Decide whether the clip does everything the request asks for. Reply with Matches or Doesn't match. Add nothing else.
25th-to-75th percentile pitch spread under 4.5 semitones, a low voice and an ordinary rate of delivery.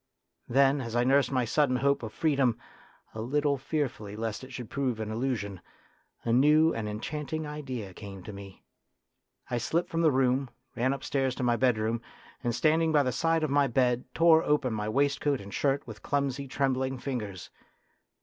Matches